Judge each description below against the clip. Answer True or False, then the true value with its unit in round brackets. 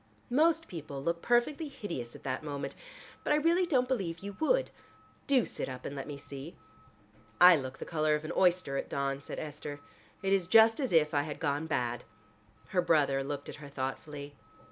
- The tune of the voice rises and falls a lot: True (7.8 semitones)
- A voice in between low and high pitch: True (155 Hz)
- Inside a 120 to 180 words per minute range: False (195 wpm)